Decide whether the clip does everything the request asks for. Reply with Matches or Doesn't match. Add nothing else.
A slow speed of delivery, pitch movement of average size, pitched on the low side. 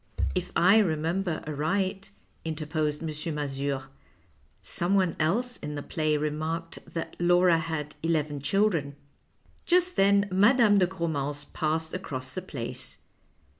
Doesn't match